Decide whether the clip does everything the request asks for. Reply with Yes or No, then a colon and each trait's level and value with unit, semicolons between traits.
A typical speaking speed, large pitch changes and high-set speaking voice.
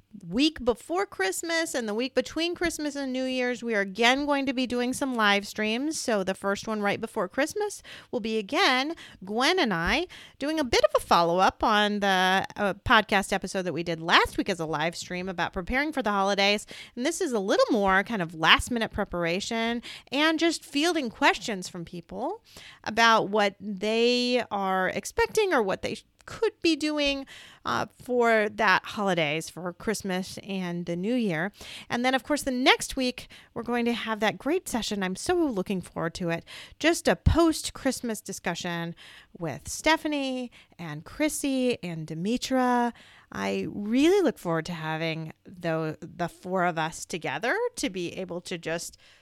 Yes: average, 180 wpm; wide, 6.8 semitones; high, 225 Hz